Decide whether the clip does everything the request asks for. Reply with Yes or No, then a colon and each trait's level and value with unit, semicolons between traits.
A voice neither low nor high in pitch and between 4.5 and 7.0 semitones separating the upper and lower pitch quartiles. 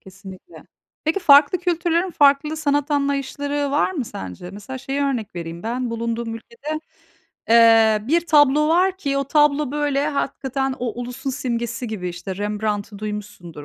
No: very high, 270 Hz; average, 5.2 semitones